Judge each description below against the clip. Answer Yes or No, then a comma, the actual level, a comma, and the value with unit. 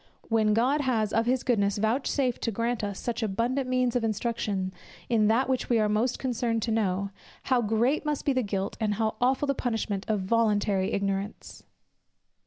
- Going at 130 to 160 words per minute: No, average, 185 wpm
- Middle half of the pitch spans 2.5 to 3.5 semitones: Yes, average, 3.1 semitones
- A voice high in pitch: Yes, high, 225 Hz